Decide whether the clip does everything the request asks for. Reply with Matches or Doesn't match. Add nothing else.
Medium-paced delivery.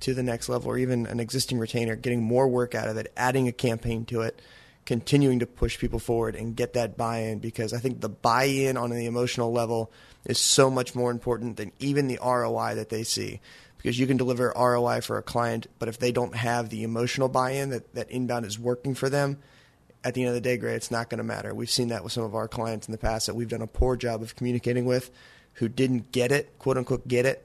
Doesn't match